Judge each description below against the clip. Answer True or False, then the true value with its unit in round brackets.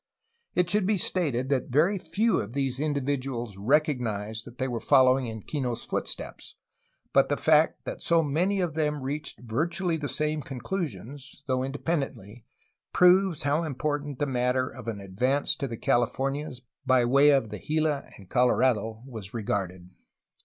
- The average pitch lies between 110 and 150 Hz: True (135 Hz)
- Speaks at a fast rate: False (160 wpm)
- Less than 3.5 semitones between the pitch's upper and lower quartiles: False (4.0 semitones)